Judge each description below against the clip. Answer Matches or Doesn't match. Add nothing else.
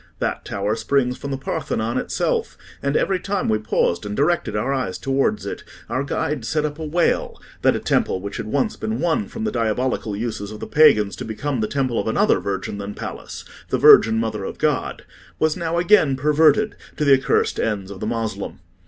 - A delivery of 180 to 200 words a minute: Matches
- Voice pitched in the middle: Doesn't match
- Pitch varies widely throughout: Matches